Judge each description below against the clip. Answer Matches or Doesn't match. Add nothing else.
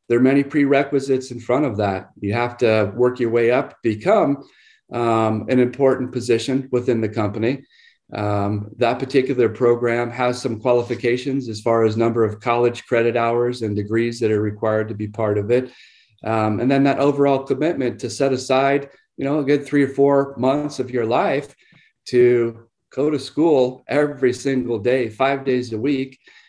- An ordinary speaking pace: Matches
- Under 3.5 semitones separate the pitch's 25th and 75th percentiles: Matches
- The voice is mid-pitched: Doesn't match